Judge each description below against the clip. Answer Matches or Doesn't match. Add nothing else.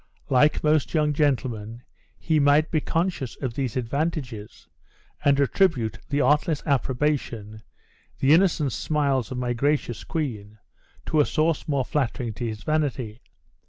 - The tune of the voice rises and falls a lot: Doesn't match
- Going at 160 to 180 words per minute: Doesn't match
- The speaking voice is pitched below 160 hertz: Matches